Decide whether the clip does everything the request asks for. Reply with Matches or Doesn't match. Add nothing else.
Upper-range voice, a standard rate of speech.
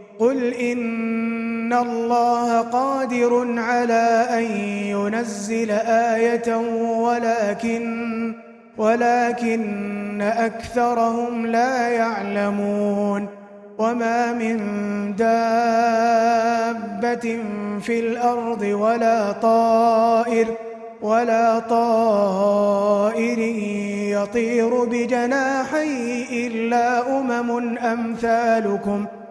Doesn't match